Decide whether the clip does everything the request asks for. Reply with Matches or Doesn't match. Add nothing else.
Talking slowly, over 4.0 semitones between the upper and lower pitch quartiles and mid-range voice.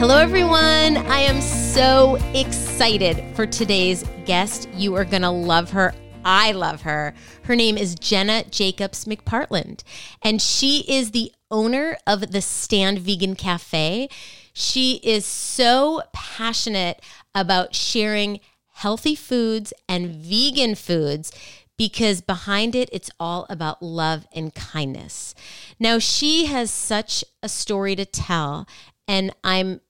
Doesn't match